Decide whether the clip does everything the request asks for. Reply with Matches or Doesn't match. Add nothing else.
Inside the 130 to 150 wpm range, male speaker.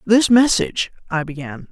Doesn't match